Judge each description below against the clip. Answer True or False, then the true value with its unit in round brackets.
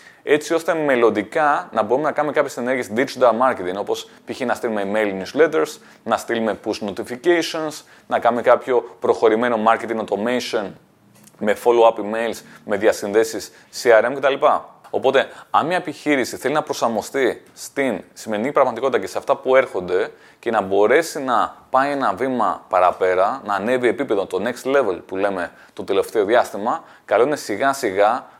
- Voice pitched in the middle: False (130 Hz)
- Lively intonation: True (6.5 semitones)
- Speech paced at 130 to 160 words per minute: True (150 wpm)